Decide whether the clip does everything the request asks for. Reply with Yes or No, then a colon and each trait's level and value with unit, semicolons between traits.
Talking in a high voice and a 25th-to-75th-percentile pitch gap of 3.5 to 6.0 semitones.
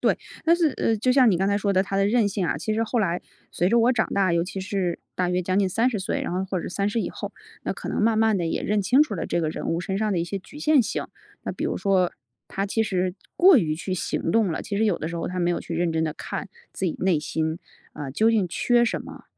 Yes: high, 195 Hz; average, 3.9 semitones